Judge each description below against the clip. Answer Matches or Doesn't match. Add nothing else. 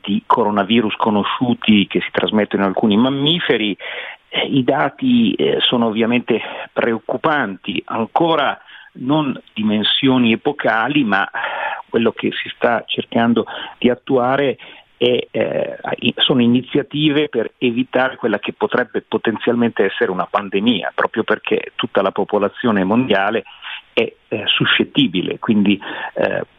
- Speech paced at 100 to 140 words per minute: Matches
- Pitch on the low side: Matches